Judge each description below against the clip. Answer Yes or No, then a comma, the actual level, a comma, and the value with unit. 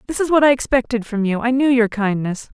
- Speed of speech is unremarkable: No, fast, 230 wpm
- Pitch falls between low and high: No, high, 240 Hz